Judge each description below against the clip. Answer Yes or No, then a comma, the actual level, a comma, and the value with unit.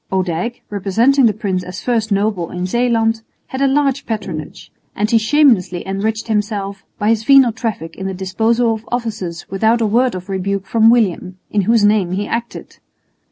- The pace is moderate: Yes, average, 175 wpm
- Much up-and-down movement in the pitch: No, average, 3.4 semitones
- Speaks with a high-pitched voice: Yes, high, 215 Hz